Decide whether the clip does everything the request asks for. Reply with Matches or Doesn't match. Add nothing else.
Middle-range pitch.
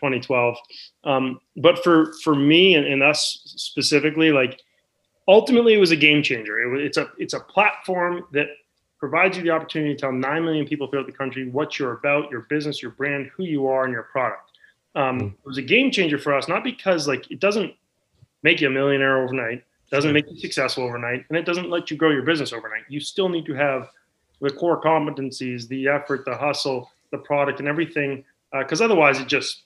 Matches